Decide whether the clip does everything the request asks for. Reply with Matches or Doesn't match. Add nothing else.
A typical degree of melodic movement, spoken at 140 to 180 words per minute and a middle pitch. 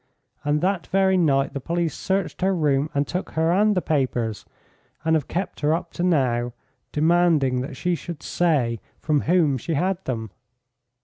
Matches